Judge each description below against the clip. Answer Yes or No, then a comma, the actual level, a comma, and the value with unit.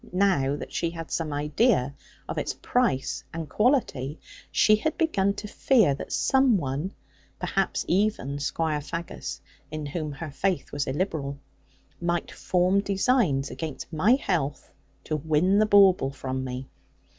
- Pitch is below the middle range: No, medium, 165 Hz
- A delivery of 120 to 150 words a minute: Yes, average, 145 wpm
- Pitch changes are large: Yes, wide, 5.8 semitones